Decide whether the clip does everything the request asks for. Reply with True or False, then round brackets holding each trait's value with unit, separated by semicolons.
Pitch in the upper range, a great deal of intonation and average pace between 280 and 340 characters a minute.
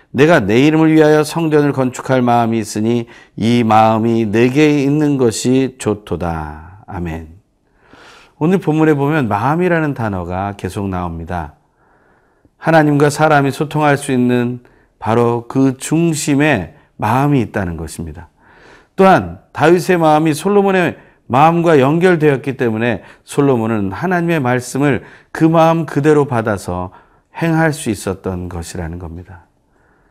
False (125 Hz; 7.1 semitones; 285 characters per minute)